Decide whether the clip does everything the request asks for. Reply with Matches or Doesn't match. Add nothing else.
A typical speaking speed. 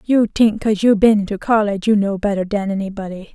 Doesn't match